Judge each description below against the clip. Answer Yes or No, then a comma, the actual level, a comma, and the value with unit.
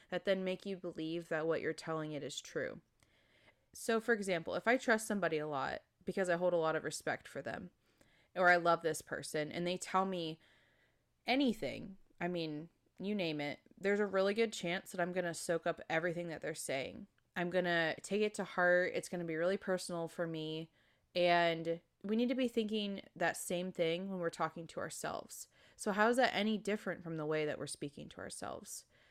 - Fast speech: Yes, fast, 210 wpm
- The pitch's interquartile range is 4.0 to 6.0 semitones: No, average, 3.6 semitones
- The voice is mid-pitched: Yes, medium, 175 Hz